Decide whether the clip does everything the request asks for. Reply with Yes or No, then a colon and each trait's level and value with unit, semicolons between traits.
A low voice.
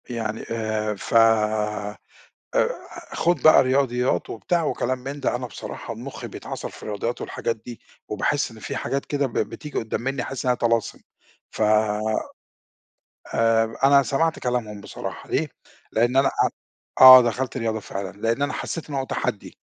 Yes: low, 125 Hz